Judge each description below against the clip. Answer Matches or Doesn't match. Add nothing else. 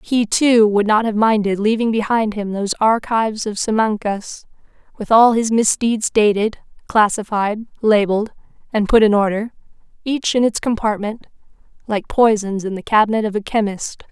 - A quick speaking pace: Doesn't match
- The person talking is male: Doesn't match